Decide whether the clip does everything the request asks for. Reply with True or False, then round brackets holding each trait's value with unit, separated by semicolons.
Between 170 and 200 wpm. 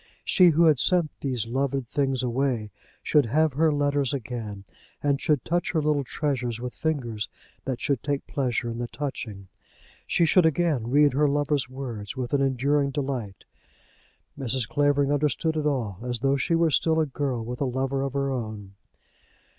True (180 wpm)